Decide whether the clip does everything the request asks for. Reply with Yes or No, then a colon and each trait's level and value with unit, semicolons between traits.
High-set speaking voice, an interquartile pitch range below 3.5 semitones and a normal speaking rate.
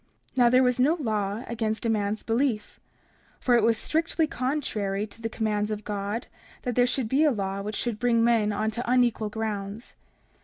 Yes: high, 225 Hz; average, 2.8 semitones; average, 195 wpm